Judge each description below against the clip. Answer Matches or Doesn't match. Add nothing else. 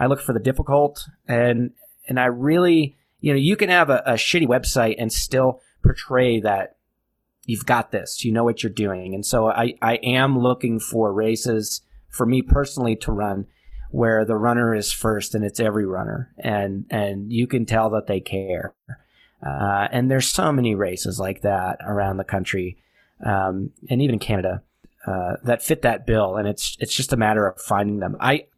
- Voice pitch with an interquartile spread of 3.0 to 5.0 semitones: Matches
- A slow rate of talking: Doesn't match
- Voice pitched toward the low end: Matches